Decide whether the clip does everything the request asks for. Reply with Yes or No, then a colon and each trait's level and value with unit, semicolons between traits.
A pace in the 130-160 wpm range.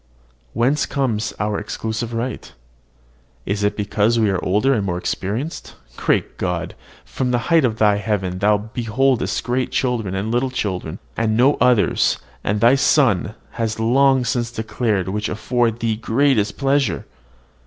Yes: average, 150 wpm